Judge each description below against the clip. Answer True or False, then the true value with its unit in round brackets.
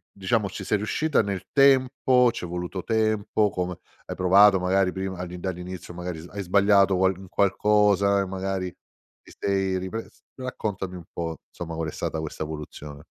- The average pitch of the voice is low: True (95 Hz)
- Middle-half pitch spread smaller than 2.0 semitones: False (2.5 semitones)